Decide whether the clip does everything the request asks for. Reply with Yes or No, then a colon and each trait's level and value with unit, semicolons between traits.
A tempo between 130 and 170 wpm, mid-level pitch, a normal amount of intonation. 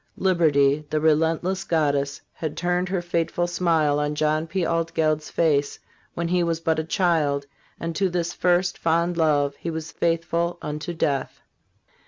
No: average, 155 wpm; medium, 165 Hz; narrow, 2.3 semitones